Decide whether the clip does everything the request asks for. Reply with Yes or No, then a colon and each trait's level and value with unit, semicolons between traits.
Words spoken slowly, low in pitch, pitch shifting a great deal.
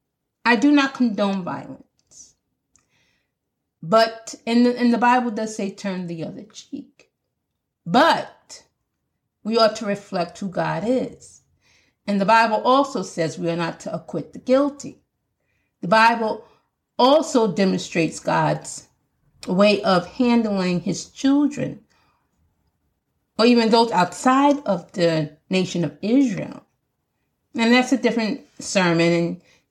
No: slow, 125 wpm; high, 210 Hz; wide, 6.0 semitones